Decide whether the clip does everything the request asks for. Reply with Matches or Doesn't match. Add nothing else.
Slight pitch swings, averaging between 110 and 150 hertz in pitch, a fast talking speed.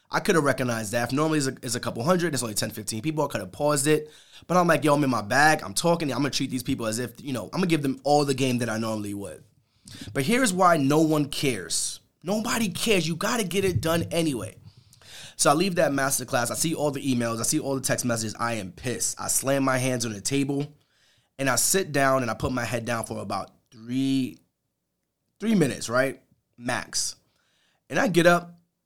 Doesn't match